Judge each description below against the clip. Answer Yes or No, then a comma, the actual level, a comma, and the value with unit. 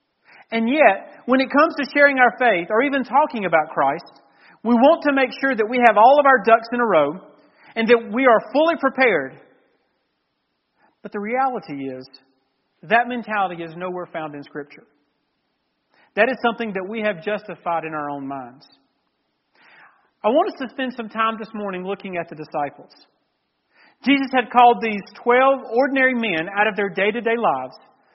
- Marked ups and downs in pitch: Yes, wide, 7.3 semitones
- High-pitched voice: Yes, high, 225 Hz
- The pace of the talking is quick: No, average, 180 wpm